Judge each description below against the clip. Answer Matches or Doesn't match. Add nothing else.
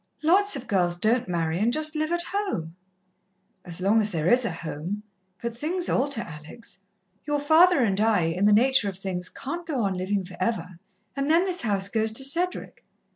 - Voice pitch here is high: Matches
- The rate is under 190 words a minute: Doesn't match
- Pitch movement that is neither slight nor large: Doesn't match